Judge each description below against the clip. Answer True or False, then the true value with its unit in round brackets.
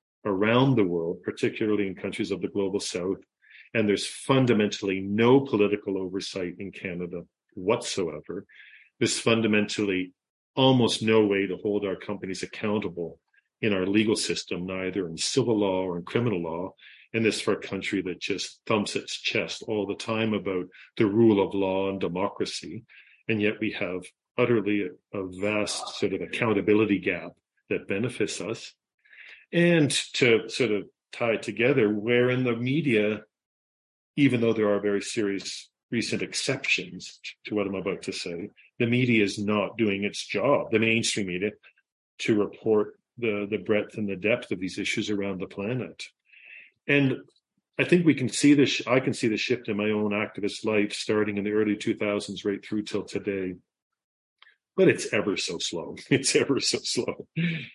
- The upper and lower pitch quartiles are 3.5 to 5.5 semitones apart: False (2.5 semitones)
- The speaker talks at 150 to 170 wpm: True (165 wpm)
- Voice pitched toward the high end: False (105 Hz)